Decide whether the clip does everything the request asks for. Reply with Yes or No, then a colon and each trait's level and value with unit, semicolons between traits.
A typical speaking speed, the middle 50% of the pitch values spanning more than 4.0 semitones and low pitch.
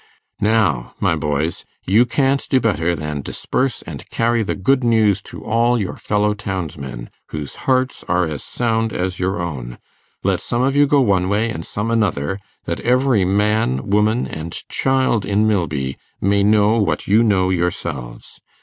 Yes: average, 165 wpm; average, 5.3 semitones; low, 100 Hz